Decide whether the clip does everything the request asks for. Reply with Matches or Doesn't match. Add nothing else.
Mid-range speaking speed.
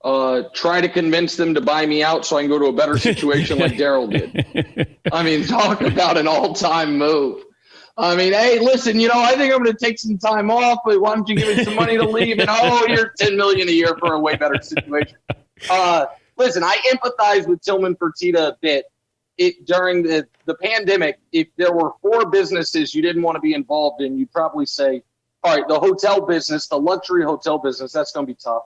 Doesn't match